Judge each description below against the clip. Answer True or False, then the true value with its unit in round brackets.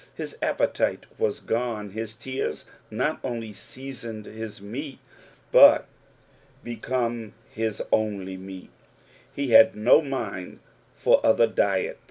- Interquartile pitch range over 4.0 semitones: False (3.2 semitones)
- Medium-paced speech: False (115 wpm)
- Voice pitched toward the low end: True (115 Hz)